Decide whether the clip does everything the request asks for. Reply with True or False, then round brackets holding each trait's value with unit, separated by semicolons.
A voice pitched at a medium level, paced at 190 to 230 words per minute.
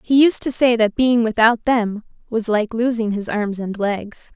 False (225 Hz; 205 wpm)